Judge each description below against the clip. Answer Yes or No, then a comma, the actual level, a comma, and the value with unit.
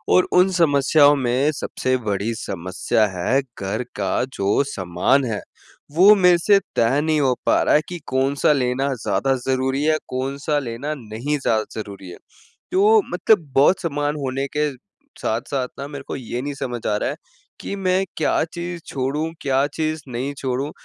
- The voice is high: No, low, 135 Hz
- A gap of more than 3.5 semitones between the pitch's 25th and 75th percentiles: Yes, average, 4.1 semitones